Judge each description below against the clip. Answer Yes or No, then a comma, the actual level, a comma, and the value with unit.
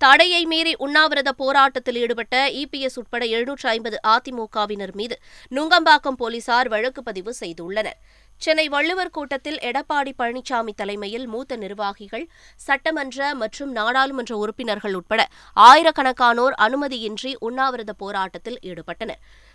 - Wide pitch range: No, average, 4.1 semitones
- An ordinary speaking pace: Yes, average, 105 wpm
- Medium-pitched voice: No, high, 245 Hz